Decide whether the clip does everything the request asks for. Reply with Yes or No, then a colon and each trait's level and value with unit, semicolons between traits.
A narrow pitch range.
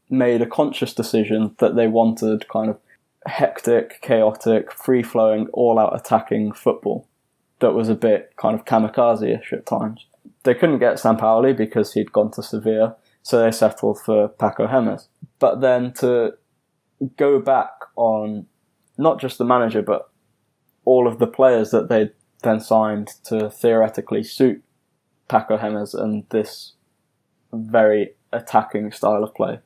Yes: narrow, 2.3 semitones